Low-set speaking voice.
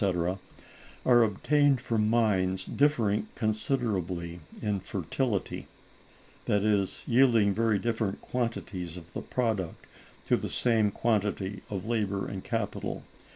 Yes: low, 105 Hz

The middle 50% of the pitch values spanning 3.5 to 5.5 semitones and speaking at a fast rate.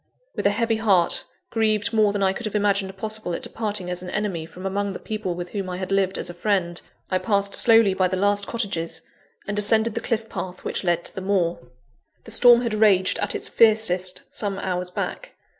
No: average, 2.9 semitones; fast, 215 wpm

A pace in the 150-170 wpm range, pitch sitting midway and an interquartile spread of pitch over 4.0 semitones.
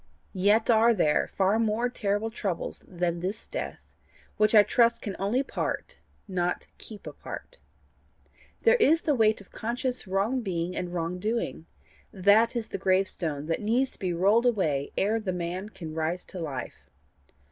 No: average, 160 wpm; high, 200 Hz; average, 4.4 semitones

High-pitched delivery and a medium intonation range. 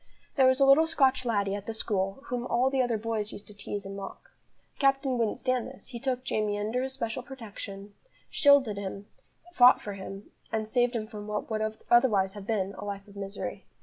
Yes: high, 220 Hz; average, 4.0 semitones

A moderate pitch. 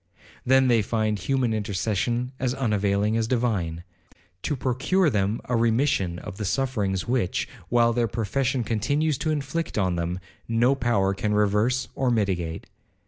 No: low, 115 Hz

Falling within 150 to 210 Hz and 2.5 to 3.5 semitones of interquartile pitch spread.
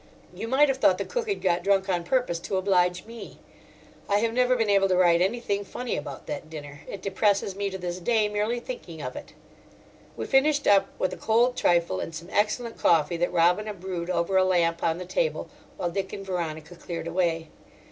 No: high, 190 Hz; average, 4.2 semitones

